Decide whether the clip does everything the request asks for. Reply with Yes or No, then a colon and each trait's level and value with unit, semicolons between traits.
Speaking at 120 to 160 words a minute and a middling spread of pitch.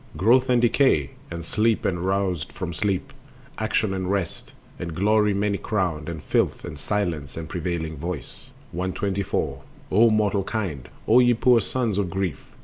Yes: average, 155 wpm; average, 4.2 semitones